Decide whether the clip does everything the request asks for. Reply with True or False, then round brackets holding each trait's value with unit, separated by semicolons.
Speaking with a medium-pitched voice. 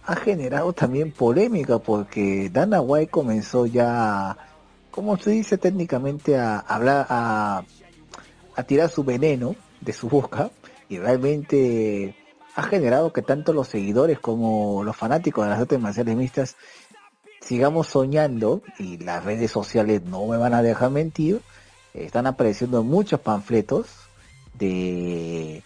False (125 Hz)